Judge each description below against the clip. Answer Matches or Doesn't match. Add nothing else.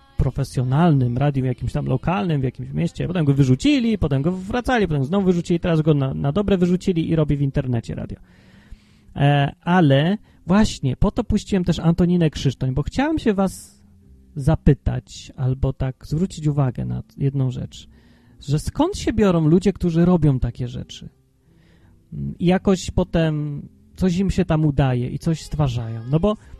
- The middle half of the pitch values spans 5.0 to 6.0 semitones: Matches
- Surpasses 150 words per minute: Matches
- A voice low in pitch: Doesn't match